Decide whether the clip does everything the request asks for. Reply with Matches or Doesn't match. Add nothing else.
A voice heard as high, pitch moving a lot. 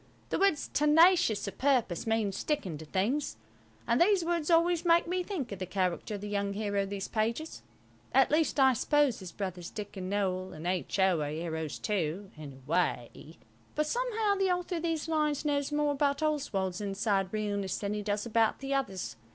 Matches